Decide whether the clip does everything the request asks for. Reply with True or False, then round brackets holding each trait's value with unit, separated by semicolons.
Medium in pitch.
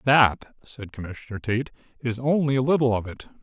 False (120 Hz)